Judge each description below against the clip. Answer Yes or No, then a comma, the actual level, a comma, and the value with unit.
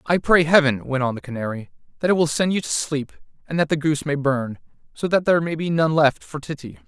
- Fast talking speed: Yes, fast, 255 wpm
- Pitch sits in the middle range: Yes, medium, 150 Hz